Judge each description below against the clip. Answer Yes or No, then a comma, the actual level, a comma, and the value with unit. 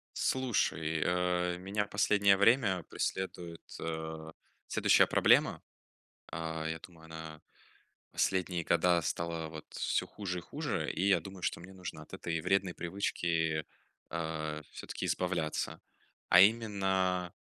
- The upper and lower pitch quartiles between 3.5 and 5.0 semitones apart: No, average, 2.9 semitones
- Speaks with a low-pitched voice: Yes, very low, 90 Hz